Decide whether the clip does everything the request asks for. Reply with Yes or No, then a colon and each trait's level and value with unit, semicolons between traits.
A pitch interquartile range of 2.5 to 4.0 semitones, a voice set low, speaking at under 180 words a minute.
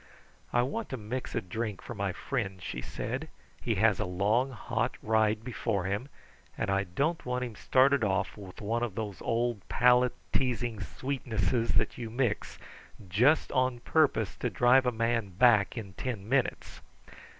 Yes: average, 3.5 semitones; low, 115 Hz; average, 165 wpm